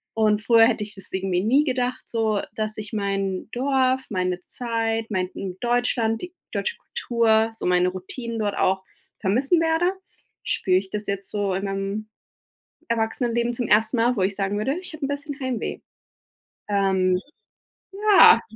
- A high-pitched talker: Yes, high, 220 Hz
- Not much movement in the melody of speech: No, average, 3.9 semitones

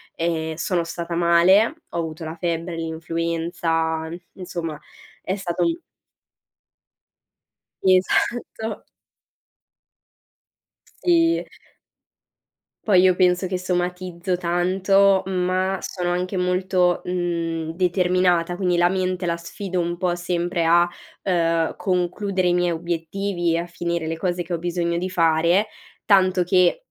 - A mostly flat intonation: Yes, narrow, 1.6 semitones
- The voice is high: No, medium, 175 Hz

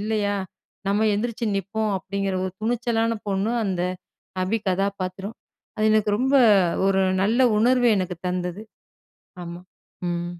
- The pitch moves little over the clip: No, average, 3.1 semitones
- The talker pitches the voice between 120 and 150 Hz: No, high, 200 Hz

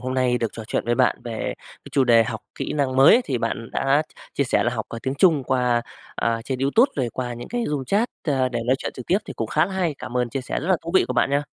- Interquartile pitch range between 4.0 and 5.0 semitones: No, average, 3.4 semitones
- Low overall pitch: Yes, low, 130 Hz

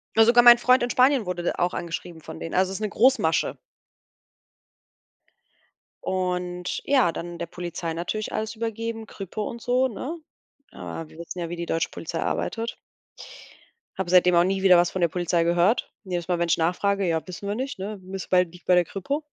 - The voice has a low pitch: No, medium, 185 Hz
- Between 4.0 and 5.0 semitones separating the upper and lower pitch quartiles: Yes, average, 4.4 semitones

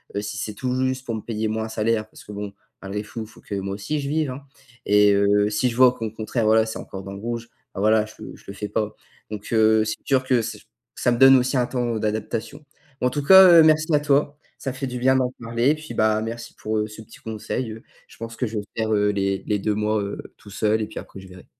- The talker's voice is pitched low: Yes, low, 110 Hz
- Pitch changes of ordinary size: Yes, average, 3.2 semitones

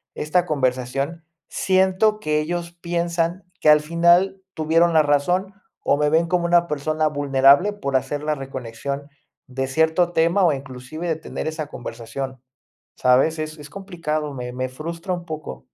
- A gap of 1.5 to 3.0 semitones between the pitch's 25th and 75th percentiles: No, average, 3.7 semitones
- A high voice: No, medium, 155 Hz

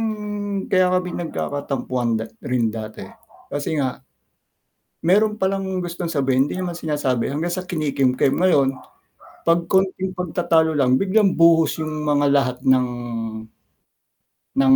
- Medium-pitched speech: Yes, medium, 155 Hz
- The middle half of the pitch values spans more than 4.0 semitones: Yes, average, 5.2 semitones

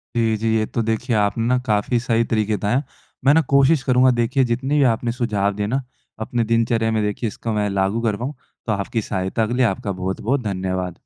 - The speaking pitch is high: No, low, 115 Hz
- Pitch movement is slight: No, average, 3.1 semitones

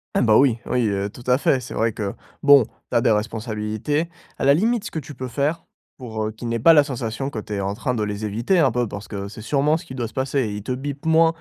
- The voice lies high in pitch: No, low, 120 Hz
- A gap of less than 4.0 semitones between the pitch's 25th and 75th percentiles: No, average, 4.7 semitones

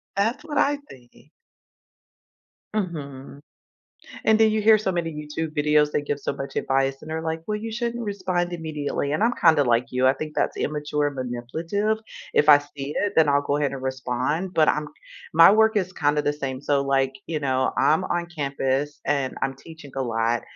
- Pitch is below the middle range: No, medium, 150 Hz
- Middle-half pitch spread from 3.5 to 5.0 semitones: Yes, average, 4.4 semitones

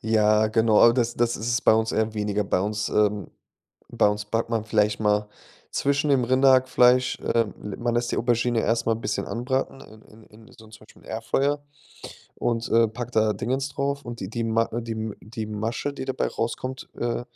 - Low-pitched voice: Yes, low, 115 Hz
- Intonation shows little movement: Yes, narrow, 2.2 semitones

